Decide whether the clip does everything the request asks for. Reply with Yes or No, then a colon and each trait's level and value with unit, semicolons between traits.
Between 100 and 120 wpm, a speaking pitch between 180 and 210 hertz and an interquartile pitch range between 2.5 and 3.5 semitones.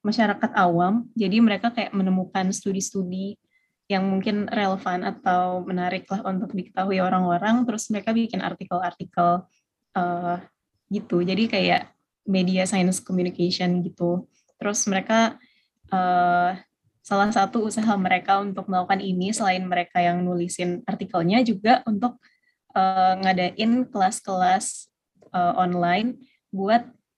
Yes: average, 115 wpm; high, 190 Hz; average, 3.0 semitones